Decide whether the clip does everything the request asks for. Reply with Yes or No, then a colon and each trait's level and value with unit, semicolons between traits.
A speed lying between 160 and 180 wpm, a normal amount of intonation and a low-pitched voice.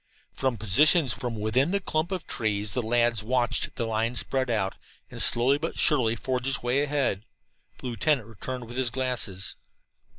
Yes: average, 165 wpm; average, 3.3 semitones; low, 125 Hz